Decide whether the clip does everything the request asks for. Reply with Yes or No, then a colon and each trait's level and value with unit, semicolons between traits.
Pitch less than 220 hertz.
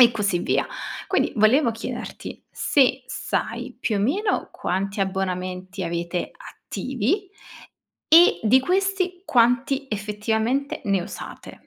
No: high, 225 Hz